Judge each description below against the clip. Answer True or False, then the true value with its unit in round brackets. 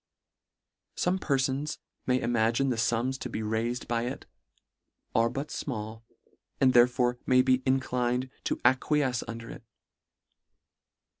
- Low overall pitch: True (125 Hz)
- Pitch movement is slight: True (2.2 semitones)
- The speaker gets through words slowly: True (125 wpm)